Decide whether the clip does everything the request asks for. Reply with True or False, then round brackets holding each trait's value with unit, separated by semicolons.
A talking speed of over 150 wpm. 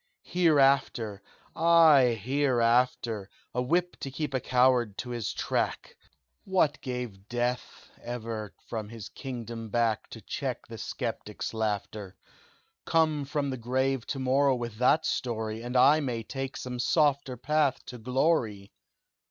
False (135 wpm)